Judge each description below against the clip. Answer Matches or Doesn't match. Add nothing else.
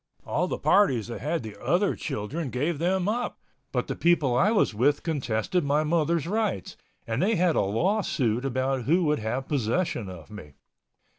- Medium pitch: Matches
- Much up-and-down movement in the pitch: Matches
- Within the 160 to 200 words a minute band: Matches